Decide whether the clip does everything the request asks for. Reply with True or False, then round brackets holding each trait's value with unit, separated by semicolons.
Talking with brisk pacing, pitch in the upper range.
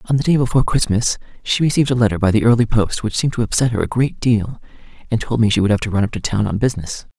False (285 wpm; 115 Hz)